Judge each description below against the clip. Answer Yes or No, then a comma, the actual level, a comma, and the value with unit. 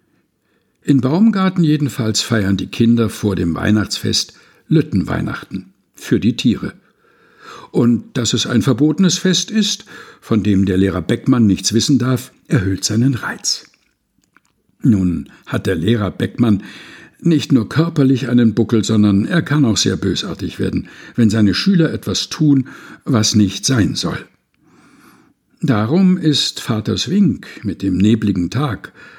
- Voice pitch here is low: Yes, low, 115 Hz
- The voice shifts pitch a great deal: Yes, wide, 5.8 semitones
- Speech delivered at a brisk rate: No, average, 135 wpm